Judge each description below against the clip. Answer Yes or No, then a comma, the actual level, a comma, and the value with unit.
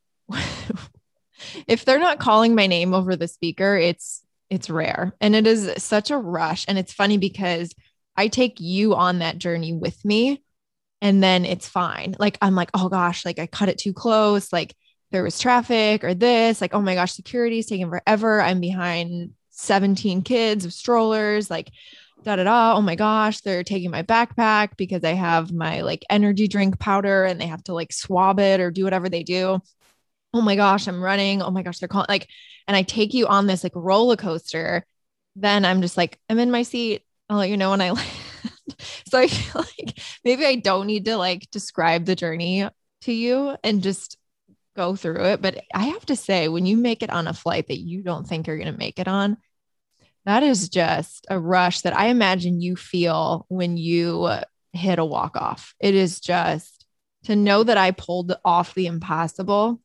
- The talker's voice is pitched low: No, high, 190 Hz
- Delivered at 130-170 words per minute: No, average, 195 wpm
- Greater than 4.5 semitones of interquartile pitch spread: No, average, 3.2 semitones